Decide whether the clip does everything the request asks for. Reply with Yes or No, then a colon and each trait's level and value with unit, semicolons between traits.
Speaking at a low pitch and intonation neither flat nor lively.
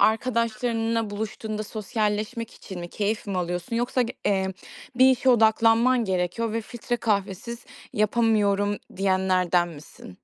No: high, 215 Hz; average, 3.1 semitones